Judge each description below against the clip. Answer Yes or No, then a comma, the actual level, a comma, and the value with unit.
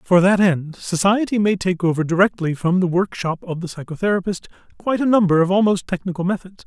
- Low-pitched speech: No, medium, 185 Hz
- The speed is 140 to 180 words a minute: No, average, 190 wpm